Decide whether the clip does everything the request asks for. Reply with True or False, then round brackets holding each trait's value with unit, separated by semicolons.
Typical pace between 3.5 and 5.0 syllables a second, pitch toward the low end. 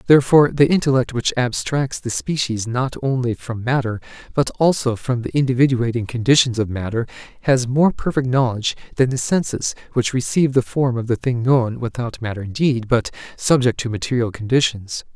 False (5.5 syllables/s; 125 Hz)